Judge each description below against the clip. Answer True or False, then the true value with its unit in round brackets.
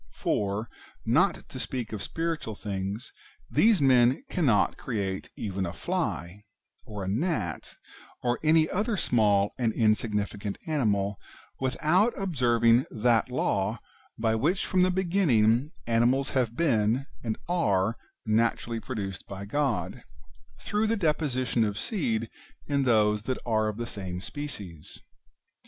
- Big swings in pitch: True (5.8 semitones)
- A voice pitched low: True (115 Hz)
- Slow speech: True (130 wpm)